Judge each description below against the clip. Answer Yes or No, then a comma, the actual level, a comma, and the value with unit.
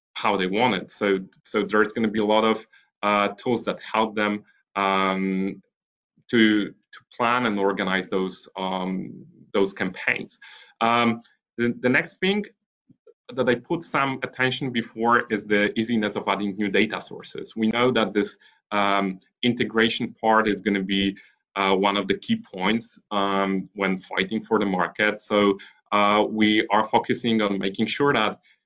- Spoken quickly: No, average, 165 wpm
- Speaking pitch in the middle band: No, low, 105 Hz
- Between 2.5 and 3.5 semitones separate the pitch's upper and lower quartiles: Yes, average, 2.8 semitones